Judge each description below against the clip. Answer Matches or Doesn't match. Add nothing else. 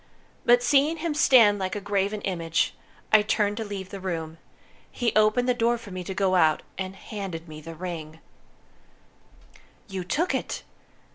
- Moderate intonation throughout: Matches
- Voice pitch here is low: Doesn't match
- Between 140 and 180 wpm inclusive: Matches